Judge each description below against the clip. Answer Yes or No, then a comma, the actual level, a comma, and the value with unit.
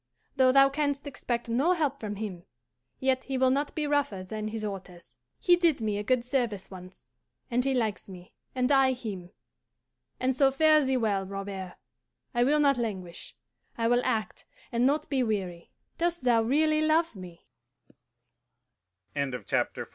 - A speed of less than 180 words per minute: Yes, average, 160 wpm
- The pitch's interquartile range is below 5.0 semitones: No, wide, 5.4 semitones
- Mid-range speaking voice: No, high, 245 Hz